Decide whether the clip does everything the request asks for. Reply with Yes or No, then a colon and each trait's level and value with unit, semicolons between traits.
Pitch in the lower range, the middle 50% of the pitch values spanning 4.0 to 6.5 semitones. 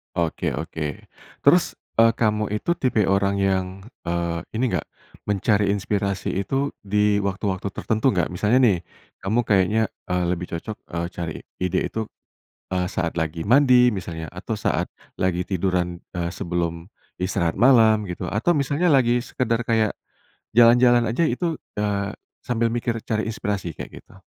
Yes: low, 100 Hz; average, 4.3 semitones